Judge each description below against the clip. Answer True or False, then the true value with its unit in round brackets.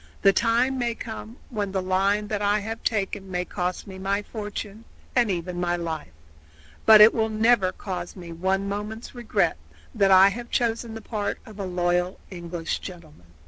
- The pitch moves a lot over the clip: False (3.4 semitones)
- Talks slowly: False (180 wpm)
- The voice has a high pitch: True (200 Hz)